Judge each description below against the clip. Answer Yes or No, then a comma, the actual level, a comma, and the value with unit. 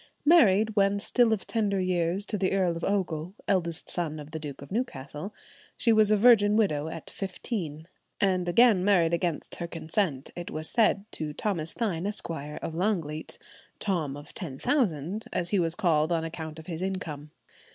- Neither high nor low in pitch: Yes, medium, 175 Hz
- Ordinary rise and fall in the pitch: Yes, average, 4.3 semitones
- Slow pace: No, average, 180 wpm